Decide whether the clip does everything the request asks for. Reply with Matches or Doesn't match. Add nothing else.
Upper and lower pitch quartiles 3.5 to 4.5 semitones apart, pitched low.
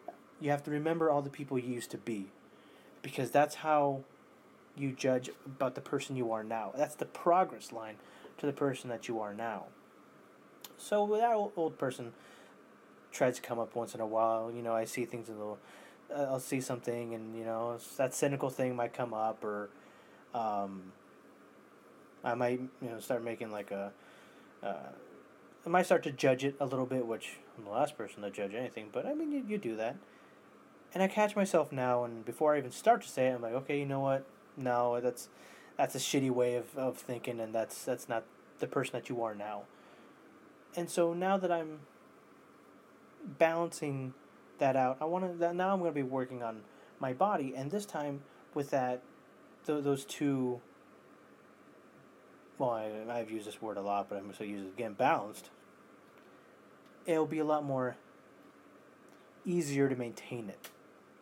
Matches